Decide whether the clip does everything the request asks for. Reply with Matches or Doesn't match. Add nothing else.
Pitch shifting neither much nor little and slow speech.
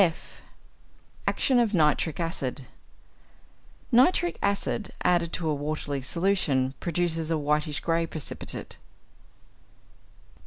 Matches